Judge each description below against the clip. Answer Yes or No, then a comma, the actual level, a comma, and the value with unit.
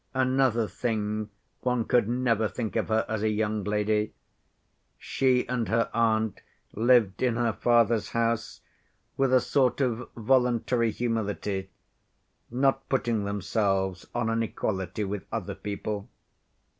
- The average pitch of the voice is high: No, low, 115 Hz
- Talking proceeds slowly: Yes, slow, 130 wpm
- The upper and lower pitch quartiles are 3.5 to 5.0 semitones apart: No, narrow, 2.6 semitones